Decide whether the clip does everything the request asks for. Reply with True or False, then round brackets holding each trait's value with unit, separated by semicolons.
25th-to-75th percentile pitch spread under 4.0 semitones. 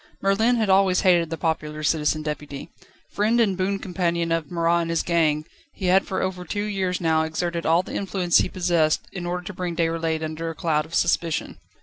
True (2.7 semitones)